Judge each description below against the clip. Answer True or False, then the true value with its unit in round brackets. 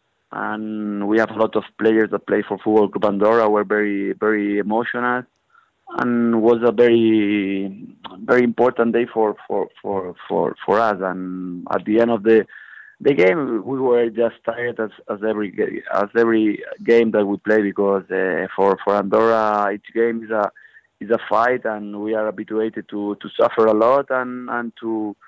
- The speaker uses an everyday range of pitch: False (2.0 semitones)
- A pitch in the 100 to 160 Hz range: True (110 Hz)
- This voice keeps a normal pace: True (175 wpm)